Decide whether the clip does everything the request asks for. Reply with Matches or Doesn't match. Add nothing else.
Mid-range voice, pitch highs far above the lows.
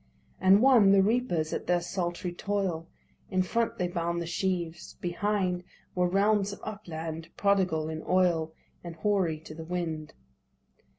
Doesn't match